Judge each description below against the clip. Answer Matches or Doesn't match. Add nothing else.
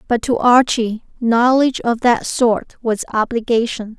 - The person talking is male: Doesn't match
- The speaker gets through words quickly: Doesn't match